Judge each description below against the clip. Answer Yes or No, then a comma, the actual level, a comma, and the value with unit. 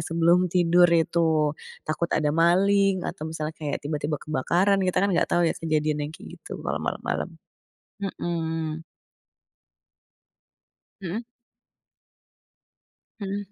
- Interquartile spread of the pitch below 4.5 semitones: Yes, average, 2.8 semitones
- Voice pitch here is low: No, medium, 165 Hz